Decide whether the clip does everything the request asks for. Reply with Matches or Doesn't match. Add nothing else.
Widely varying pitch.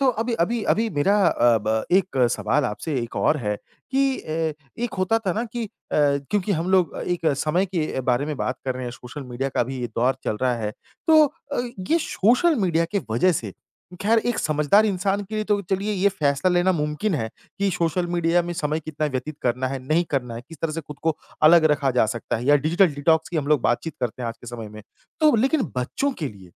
Matches